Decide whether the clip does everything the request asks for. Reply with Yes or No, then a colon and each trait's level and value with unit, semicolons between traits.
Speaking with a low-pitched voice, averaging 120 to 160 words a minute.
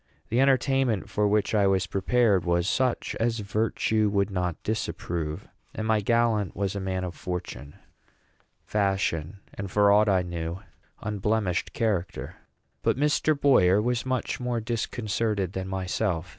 Yes: low, 100 Hz; average, 145 wpm